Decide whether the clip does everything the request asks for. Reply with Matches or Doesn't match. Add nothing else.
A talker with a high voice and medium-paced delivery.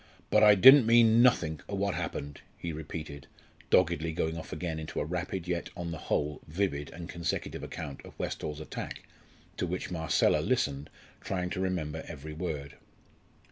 Doesn't match